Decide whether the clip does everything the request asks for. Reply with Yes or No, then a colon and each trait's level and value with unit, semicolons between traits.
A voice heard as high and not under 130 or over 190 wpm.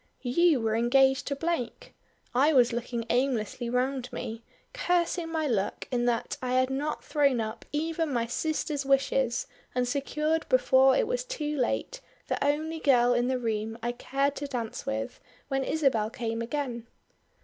Yes: very high, 265 Hz; average, 160 wpm